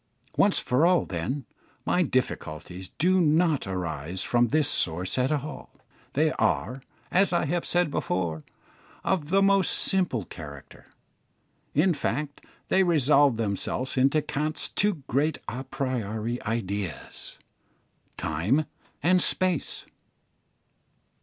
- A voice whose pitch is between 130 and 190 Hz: Yes, low, 135 Hz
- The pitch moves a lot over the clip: Yes, wide, 8.4 semitones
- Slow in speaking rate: Yes, slow, 115 wpm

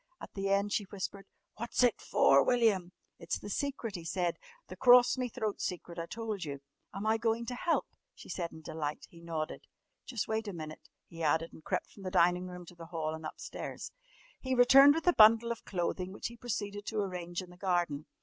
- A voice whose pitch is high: Yes, high, 195 Hz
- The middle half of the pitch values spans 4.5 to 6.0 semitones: Yes, average, 4.9 semitones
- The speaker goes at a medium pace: No, fast, 215 wpm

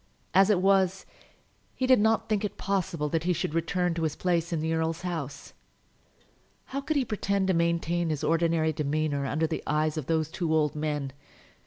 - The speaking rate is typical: Yes, average, 190 wpm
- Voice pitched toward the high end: No, medium, 165 Hz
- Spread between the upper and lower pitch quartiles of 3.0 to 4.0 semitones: Yes, average, 3.4 semitones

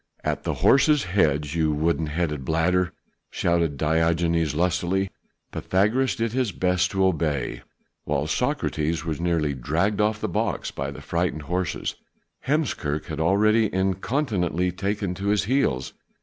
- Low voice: Yes, very low, 90 Hz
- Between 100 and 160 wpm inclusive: Yes, slow, 135 wpm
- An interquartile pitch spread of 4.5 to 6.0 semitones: No, average, 4.0 semitones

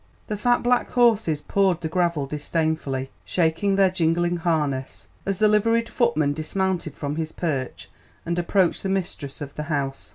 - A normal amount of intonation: Yes, average, 4.6 semitones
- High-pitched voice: No, medium, 170 Hz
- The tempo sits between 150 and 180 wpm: Yes, average, 160 wpm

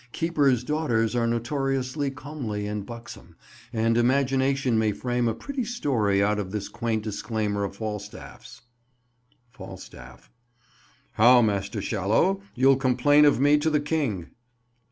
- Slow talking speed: Yes, slow, 130 wpm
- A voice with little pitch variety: No, average, 4.8 semitones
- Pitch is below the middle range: Yes, low, 120 Hz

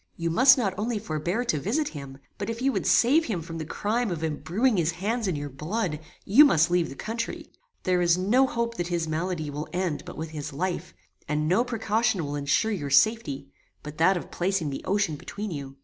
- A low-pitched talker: No, medium, 180 Hz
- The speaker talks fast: Yes, fast, 215 wpm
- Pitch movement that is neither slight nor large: No, wide, 6.2 semitones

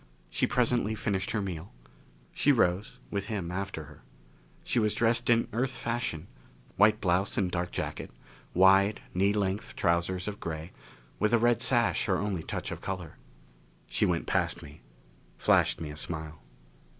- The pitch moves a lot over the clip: No, average, 3.6 semitones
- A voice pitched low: Yes, very low, 95 Hz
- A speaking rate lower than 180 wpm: Yes, average, 160 wpm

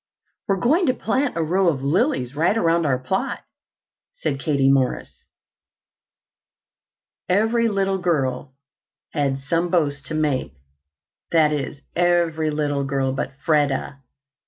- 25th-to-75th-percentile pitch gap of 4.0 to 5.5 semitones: Yes, average, 5.1 semitones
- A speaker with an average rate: No, slow, 125 wpm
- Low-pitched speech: No, medium, 155 Hz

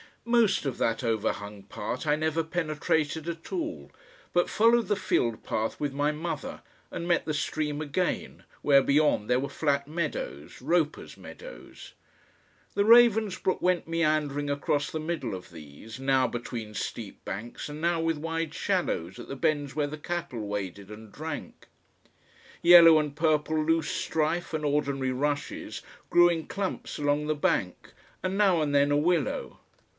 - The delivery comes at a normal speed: Yes, average, 155 wpm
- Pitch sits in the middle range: Yes, medium, 150 Hz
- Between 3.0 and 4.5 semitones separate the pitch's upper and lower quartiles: Yes, average, 3.7 semitones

